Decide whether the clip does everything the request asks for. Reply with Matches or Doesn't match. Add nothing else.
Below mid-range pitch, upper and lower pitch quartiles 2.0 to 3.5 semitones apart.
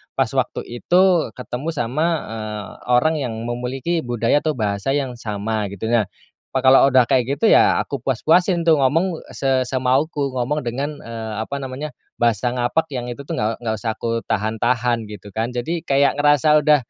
Doesn't match